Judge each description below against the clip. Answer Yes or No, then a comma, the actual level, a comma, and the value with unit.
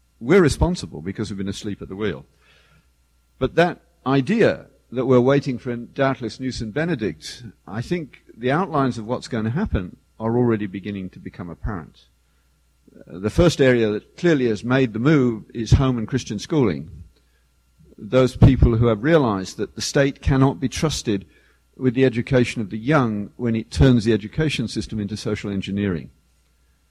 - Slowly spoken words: No, average, 170 wpm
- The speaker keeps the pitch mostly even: No, average, 4.6 semitones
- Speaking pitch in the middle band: No, low, 115 Hz